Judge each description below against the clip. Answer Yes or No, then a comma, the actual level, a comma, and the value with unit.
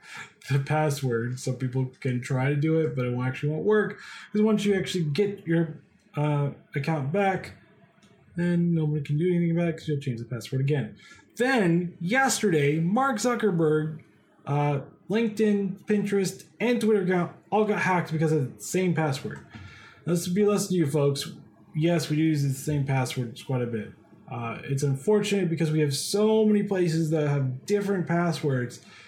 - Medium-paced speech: Yes, average, 170 wpm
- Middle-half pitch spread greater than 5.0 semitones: Yes, wide, 5.6 semitones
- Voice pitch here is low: No, medium, 165 Hz